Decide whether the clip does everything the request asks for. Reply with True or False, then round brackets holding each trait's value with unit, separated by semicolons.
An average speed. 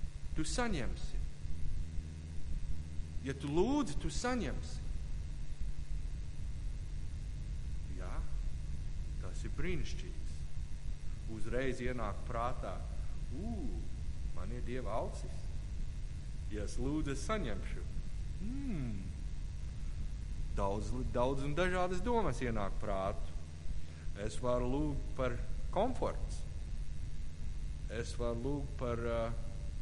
False (75 wpm)